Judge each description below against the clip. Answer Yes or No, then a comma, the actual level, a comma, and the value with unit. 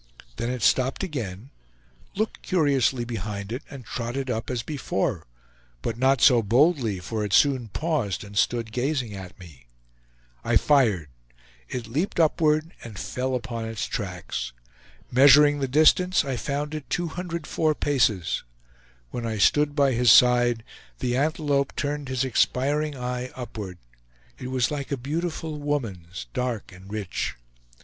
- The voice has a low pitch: Yes, low, 125 Hz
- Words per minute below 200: Yes, average, 140 wpm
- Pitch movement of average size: Yes, average, 4.6 semitones